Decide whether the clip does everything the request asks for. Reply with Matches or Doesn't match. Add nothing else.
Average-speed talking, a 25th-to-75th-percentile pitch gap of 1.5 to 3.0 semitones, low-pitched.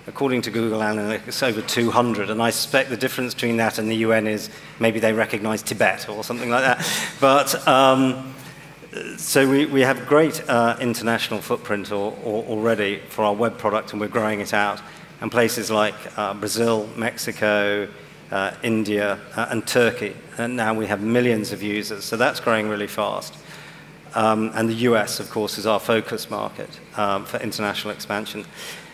Matches